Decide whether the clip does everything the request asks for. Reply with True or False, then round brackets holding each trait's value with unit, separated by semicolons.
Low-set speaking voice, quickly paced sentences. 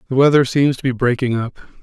True (130 Hz; 230 wpm)